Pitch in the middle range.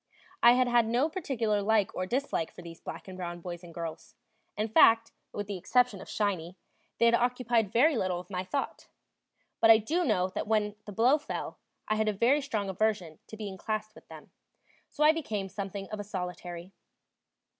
No: high, 210 Hz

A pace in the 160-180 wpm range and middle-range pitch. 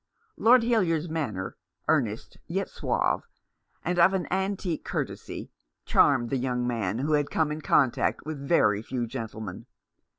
No: average, 140 wpm; medium, 145 Hz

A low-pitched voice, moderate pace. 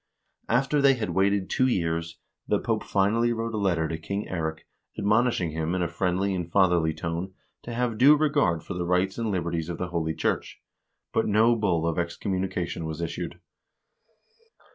Yes: very low, 95 Hz; average, 175 wpm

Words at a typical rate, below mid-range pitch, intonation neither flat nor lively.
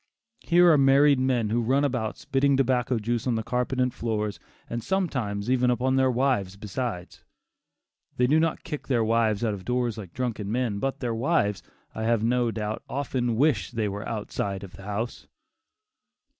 Yes: average, 180 wpm; low, 120 Hz; average, 3.5 semitones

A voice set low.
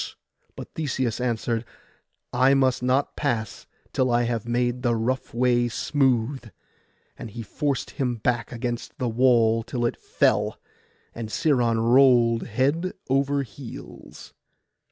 Yes: low, 120 Hz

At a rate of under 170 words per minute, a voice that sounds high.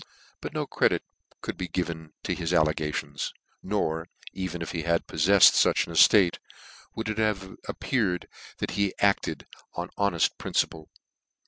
No: average, 150 wpm; very low, 90 Hz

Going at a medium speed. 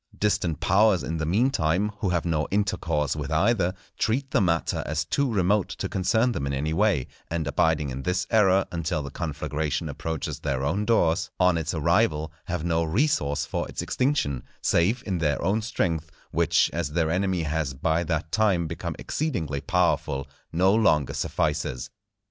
Yes: average, 170 wpm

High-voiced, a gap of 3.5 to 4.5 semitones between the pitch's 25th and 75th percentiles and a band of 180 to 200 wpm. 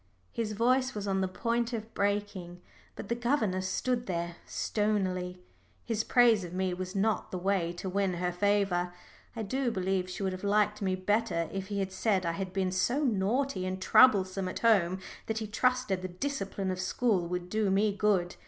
No: high, 195 Hz; average, 3.0 semitones; average, 190 wpm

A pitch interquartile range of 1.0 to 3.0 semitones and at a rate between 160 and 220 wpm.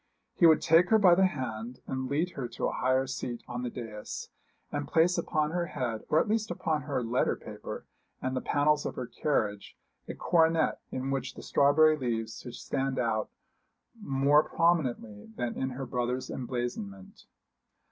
No: average, 4.5 semitones; average, 175 wpm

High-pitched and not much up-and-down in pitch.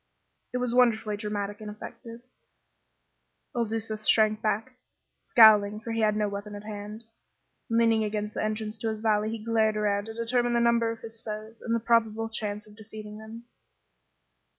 Yes: high, 220 Hz; narrow, 1.3 semitones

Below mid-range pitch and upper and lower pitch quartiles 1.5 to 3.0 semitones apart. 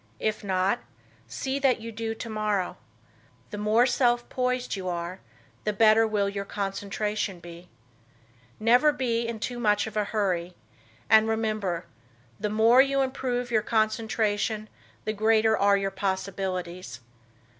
No: high, 215 Hz; average, 2.7 semitones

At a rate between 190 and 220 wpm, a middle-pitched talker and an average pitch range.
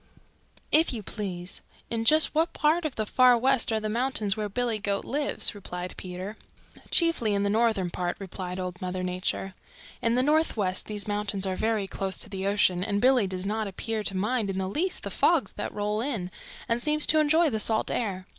No: average, 200 wpm; high, 210 Hz; average, 4.4 semitones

